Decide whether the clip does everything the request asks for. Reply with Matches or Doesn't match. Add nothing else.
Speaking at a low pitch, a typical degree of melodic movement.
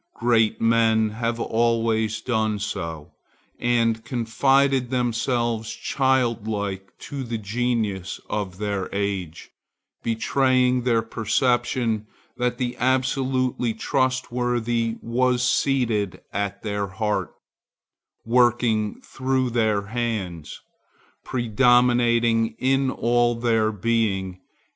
Doesn't match